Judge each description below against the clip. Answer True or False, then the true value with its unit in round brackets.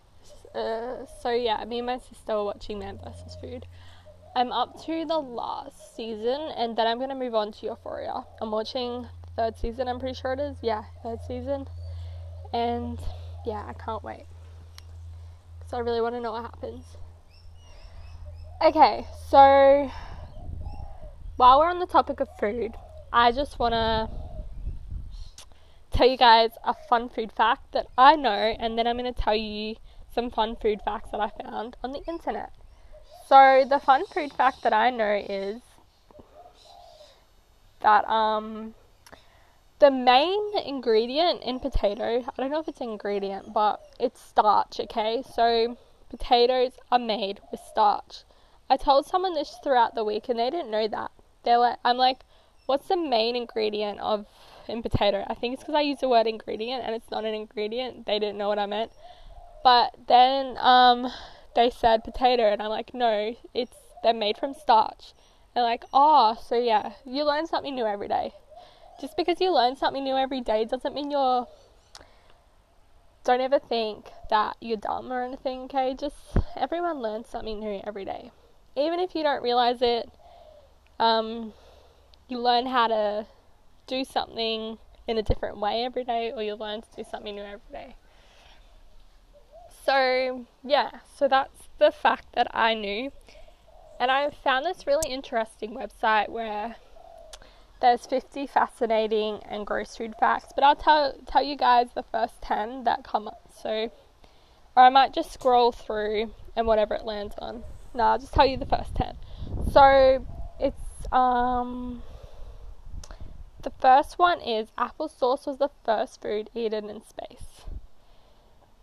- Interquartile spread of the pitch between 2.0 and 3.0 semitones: False (4.2 semitones)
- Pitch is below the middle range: False (240 Hz)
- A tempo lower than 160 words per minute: False (165 wpm)